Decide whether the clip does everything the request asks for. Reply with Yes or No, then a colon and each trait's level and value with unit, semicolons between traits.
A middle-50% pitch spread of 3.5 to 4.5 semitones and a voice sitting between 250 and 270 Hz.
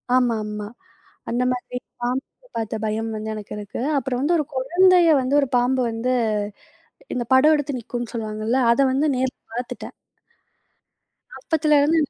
Yes: average, 4.1 semitones; very high, 255 Hz